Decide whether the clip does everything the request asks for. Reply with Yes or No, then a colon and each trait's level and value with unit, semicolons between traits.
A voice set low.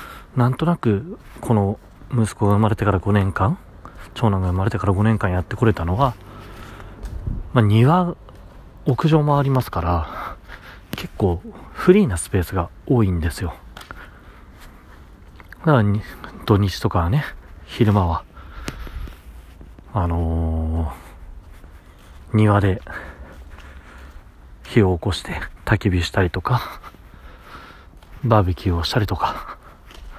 Yes: very low, 95 Hz